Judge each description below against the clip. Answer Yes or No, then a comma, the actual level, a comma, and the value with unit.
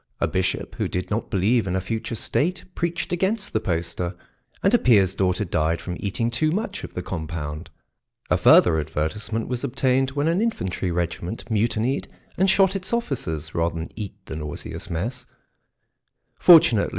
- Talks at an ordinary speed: Yes, average, 165 wpm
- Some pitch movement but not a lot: No, wide, 8.3 semitones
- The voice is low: Yes, low, 105 Hz